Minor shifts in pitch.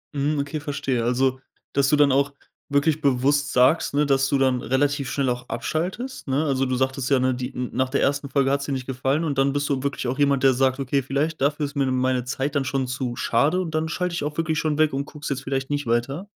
Yes: narrow, 1.9 semitones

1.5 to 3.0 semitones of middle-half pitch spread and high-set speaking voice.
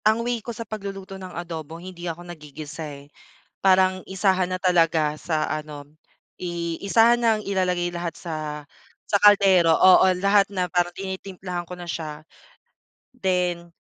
No: narrow, 2.6 semitones; medium, 180 Hz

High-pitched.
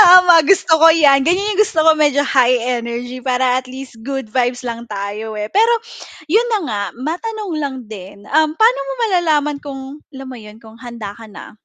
Yes: very high, 270 Hz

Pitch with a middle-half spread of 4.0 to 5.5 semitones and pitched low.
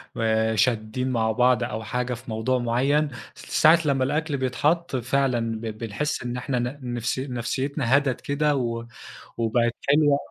No: average, 3.2 semitones; low, 125 Hz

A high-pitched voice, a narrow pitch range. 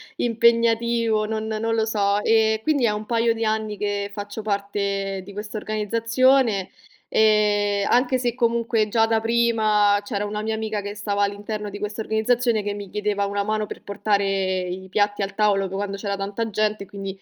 Yes: high, 210 Hz; narrow, 1.8 semitones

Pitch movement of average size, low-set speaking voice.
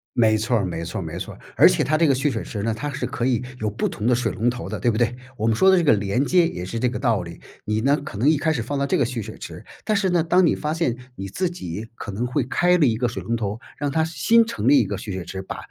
No: wide, 5.9 semitones; low, 120 Hz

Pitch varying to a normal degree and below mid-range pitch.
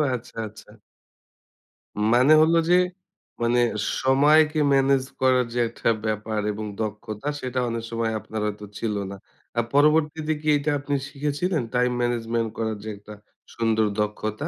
Yes: average, 4.6 semitones; low, 120 Hz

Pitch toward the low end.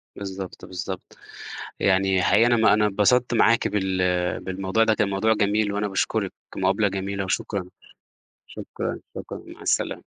Yes: low, 100 Hz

